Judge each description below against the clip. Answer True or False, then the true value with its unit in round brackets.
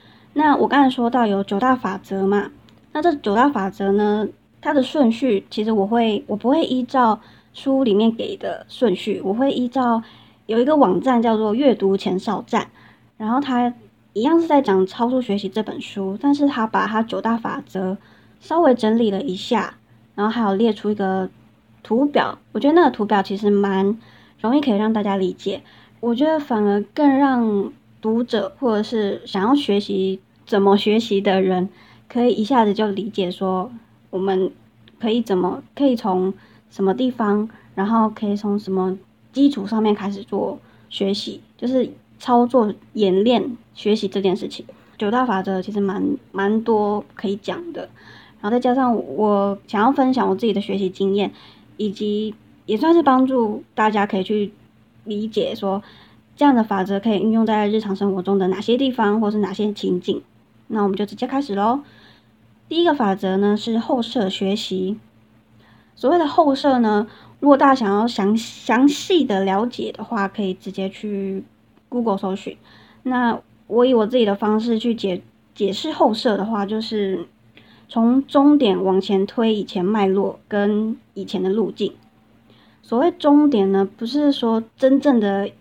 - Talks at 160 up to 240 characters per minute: False (250 characters per minute)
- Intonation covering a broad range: False (3.8 semitones)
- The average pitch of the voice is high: True (210 Hz)